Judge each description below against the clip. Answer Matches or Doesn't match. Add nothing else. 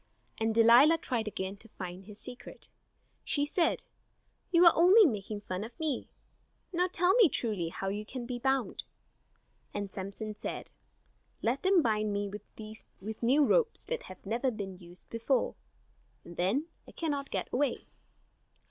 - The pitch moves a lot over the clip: Matches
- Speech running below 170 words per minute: Matches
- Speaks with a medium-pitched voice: Doesn't match